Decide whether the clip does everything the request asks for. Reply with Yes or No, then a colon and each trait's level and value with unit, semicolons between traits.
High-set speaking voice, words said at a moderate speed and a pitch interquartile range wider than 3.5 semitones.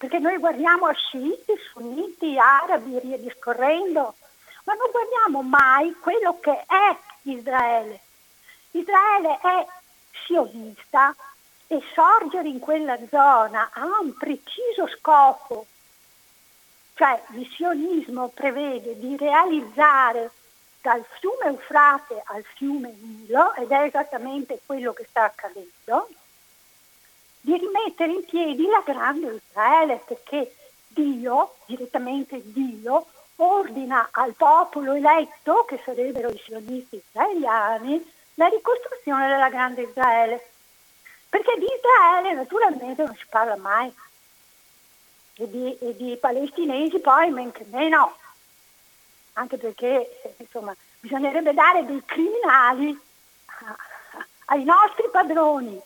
No: very high, 280 Hz; slow, 105 wpm; average, 5.3 semitones